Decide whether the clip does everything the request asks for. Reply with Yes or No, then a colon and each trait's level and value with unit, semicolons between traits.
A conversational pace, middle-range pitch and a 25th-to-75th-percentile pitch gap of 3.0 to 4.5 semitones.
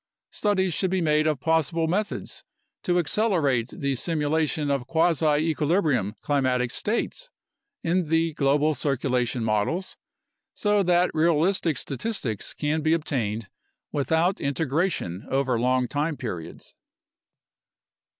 No: slow, 115 wpm; medium, 155 Hz; average, 4.2 semitones